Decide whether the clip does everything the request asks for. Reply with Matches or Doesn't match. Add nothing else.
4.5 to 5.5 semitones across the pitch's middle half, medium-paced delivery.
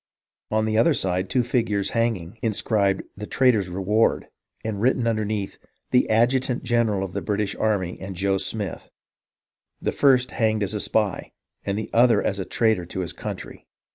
Doesn't match